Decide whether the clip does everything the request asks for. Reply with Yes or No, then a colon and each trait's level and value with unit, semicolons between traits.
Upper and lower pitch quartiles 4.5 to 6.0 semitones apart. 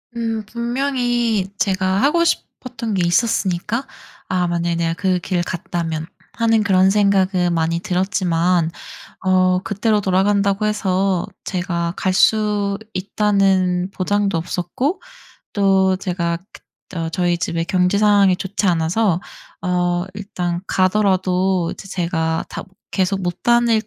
No: average, 2.7 semitones